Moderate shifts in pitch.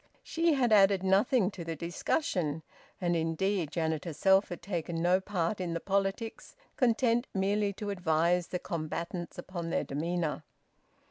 Yes: average, 3.2 semitones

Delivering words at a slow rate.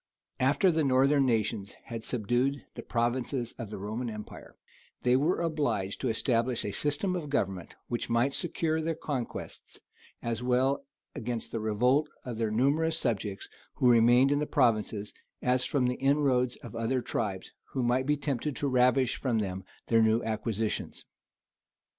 No: average, 160 wpm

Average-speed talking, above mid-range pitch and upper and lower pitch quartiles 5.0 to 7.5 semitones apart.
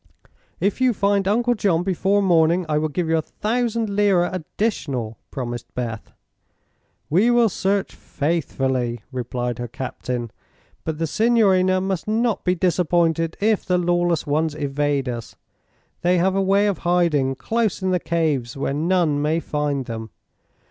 No: average, 150 wpm; medium, 170 Hz; wide, 5.5 semitones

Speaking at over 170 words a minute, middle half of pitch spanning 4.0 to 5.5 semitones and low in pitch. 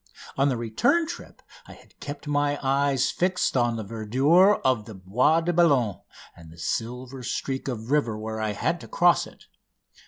Yes: average, 180 wpm; average, 4.6 semitones; low, 130 Hz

